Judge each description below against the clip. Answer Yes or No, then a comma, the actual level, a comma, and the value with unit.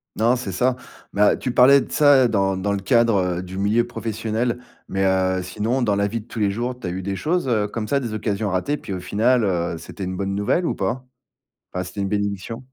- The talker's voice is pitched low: Yes, low, 105 Hz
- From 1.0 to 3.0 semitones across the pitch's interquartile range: No, average, 3.8 semitones